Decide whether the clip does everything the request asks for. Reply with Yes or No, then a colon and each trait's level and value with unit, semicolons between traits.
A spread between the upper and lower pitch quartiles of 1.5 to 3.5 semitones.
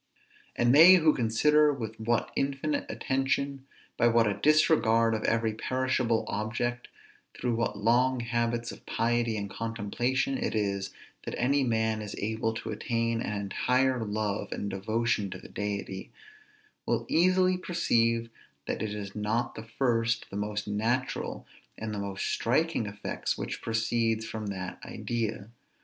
Yes: average, 3.0 semitones